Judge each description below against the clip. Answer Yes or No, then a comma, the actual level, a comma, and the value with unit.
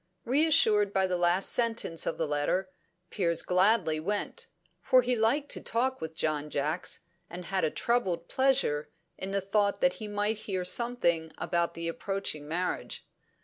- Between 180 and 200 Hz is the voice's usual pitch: Yes, high, 190 Hz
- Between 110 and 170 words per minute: Yes, average, 160 wpm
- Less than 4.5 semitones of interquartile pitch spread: No, average, 5.1 semitones